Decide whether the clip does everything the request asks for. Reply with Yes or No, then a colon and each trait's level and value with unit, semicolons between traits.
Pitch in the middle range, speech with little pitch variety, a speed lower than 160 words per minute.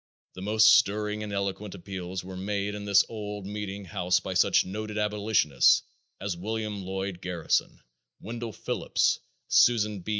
No: low, 100 Hz; narrow, 2.1 semitones; average, 145 wpm